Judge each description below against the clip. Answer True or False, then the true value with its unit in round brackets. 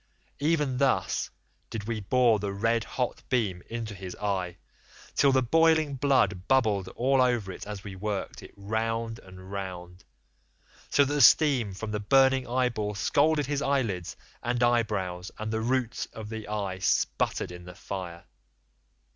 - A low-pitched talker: True (110 Hz)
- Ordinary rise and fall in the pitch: True (4.9 semitones)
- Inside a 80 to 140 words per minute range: False (155 wpm)